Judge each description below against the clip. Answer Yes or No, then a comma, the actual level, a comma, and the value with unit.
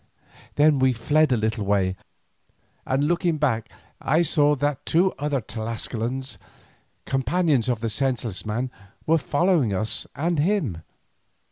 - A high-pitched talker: No, low, 135 Hz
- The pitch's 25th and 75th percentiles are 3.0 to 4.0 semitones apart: No, average, 5.1 semitones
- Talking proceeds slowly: Yes, slow, 130 wpm